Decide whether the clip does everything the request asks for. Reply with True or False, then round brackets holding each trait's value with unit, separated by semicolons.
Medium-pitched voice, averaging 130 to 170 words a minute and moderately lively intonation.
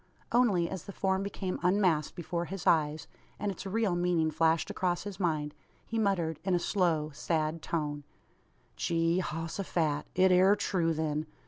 True (175 Hz; 165 wpm; 3.0 semitones)